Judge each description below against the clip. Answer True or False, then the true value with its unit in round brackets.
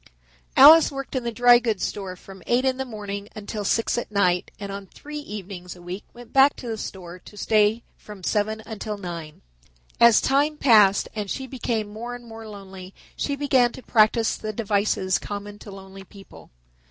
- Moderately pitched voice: False (215 Hz)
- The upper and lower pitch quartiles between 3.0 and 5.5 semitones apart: True (3.6 semitones)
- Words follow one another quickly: False (190 wpm)